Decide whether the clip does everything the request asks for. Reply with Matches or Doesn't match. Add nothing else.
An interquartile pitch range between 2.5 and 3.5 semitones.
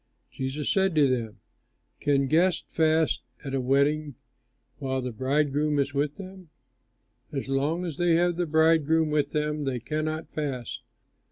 Matches